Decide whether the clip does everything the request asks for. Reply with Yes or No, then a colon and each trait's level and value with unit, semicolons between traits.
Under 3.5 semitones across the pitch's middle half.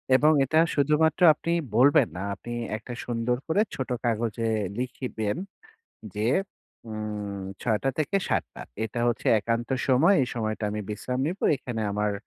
No: average, 4.2 semitones